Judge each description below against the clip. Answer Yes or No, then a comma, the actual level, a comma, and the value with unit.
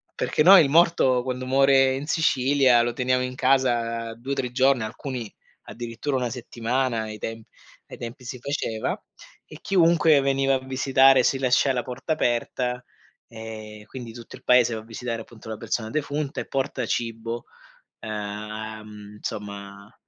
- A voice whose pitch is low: Yes, low, 125 Hz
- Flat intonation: No, average, 3.0 semitones